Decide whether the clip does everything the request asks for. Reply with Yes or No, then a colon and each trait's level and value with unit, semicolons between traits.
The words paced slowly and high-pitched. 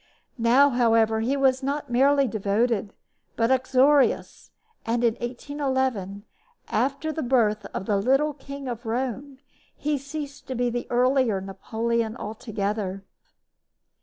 Yes: slow, 125 wpm; high, 245 Hz